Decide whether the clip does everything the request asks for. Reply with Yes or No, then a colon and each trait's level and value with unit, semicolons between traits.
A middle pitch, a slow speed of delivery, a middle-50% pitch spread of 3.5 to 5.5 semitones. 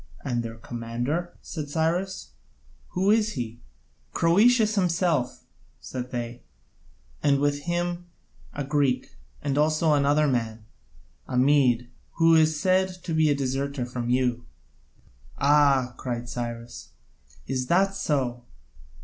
Yes: medium, 145 Hz; slow, 120 wpm; average, 5.1 semitones